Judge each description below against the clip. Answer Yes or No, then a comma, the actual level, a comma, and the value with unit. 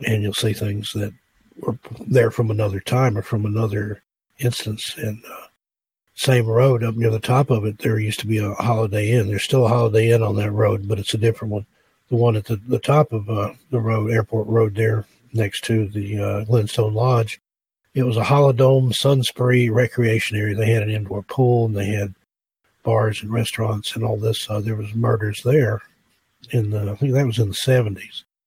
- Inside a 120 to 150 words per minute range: No, fast, 205 wpm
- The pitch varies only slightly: Yes, narrow, 2.3 semitones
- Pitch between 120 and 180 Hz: No, low, 110 Hz